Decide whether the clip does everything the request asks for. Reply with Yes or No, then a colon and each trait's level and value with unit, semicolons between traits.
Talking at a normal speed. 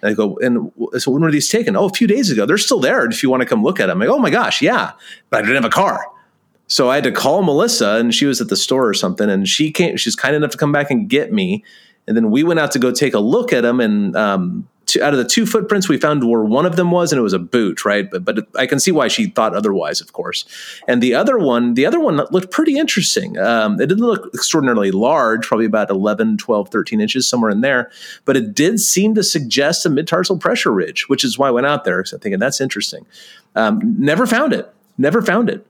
No: fast, 265 wpm